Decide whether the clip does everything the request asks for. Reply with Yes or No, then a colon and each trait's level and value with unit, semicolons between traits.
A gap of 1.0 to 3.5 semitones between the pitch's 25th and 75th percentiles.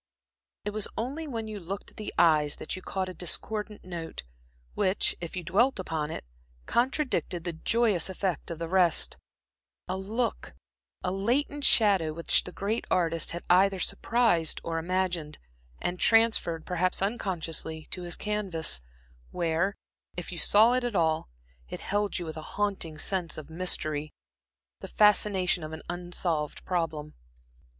No: average, 4.1 semitones